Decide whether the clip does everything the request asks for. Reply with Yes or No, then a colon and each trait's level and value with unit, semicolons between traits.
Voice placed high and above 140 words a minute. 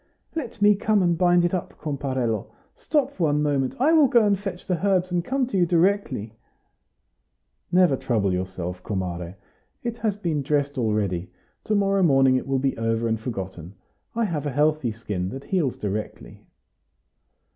No: medium, 150 Hz; average, 170 wpm